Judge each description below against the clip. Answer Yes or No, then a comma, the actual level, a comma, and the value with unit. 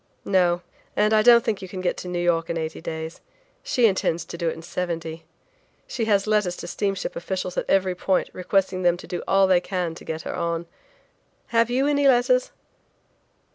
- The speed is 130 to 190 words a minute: No, average, 200 wpm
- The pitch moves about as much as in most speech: Yes, average, 3.7 semitones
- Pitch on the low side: No, medium, 185 Hz